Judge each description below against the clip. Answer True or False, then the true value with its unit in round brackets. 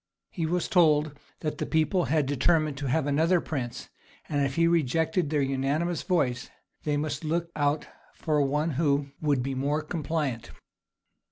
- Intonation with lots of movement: False (2.6 semitones)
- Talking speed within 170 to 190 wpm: False (160 wpm)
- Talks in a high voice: False (150 Hz)